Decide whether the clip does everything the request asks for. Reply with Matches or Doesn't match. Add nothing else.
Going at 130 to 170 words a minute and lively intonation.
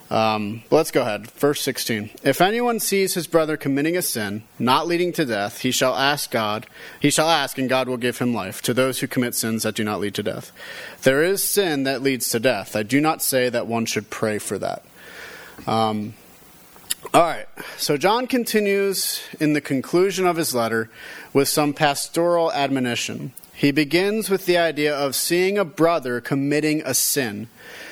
Doesn't match